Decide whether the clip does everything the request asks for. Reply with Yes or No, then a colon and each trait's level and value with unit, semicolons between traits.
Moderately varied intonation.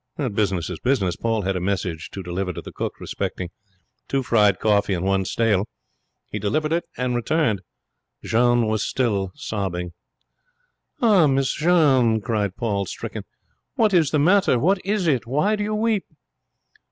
No: wide, 7.6 semitones